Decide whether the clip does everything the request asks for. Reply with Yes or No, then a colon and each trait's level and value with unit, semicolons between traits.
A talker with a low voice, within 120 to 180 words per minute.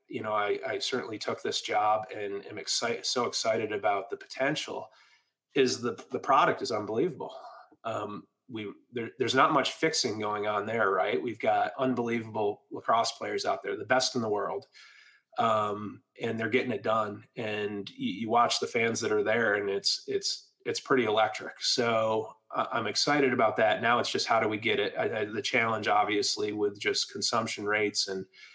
No: low, 115 Hz; average, 190 wpm